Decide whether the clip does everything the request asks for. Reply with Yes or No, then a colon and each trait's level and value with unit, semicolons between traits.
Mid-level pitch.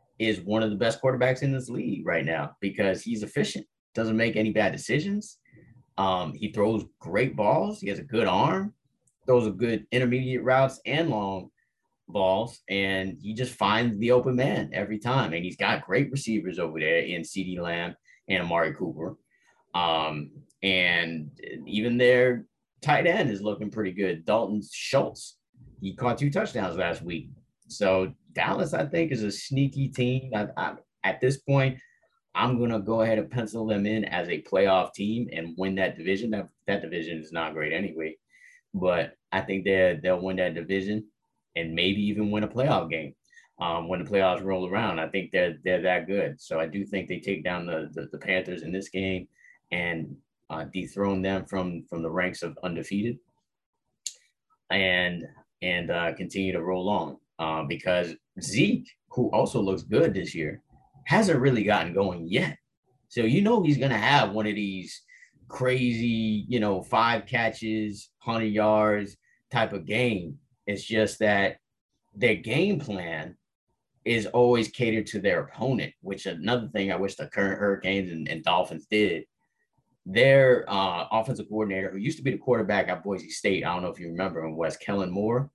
No: low, 105 Hz